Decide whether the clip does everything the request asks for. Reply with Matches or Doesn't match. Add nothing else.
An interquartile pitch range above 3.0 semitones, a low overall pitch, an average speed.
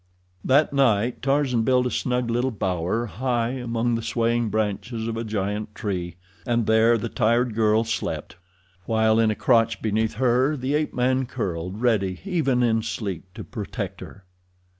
Doesn't match